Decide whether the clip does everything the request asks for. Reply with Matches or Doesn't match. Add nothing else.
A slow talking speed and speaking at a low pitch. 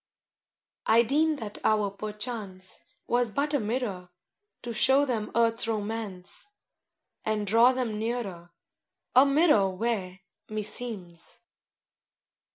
Doesn't match